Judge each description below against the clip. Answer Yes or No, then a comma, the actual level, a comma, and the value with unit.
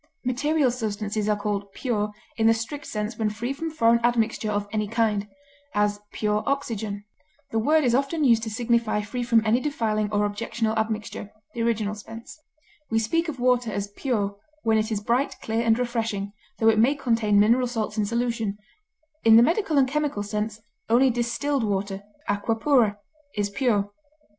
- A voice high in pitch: Yes, high, 225 Hz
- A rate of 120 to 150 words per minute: No, average, 175 wpm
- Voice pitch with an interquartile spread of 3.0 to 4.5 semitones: No, narrow, 2.6 semitones